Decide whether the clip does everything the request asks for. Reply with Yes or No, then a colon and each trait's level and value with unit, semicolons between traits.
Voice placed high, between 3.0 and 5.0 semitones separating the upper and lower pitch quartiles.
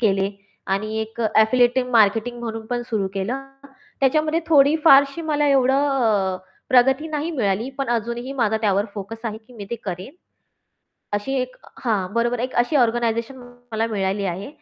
Yes: high, 235 Hz; average, 3.7 semitones